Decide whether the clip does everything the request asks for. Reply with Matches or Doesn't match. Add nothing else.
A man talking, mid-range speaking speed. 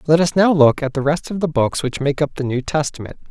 Doesn't match